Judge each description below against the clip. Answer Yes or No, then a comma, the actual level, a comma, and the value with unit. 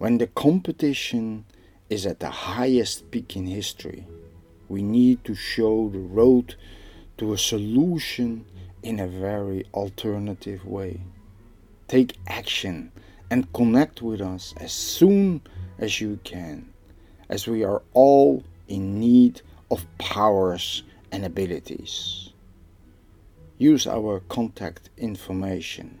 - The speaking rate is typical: No, slow, 115 wpm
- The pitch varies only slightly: No, average, 3.8 semitones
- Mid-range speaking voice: No, low, 100 Hz